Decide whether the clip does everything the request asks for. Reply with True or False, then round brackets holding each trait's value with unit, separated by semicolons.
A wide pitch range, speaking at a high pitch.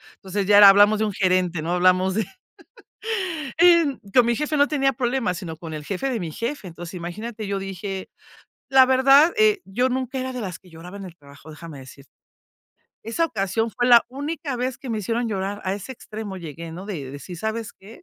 True (5.8 semitones; 205 Hz)